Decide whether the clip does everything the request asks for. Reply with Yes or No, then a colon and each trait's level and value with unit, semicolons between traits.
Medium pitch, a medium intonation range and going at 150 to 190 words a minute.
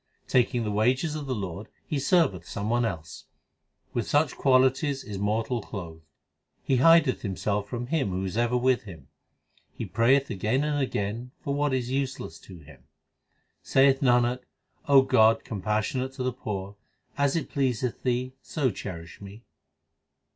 No: low, 120 Hz; average, 4.7 semitones; average, 155 wpm